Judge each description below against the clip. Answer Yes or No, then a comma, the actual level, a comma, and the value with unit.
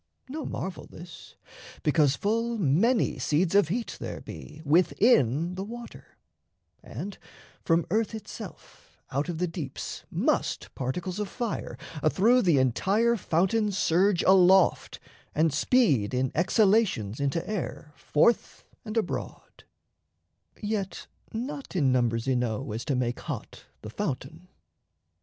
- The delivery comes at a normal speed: No, slow, 125 wpm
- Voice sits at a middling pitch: Yes, medium, 180 Hz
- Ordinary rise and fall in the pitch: No, wide, 7.1 semitones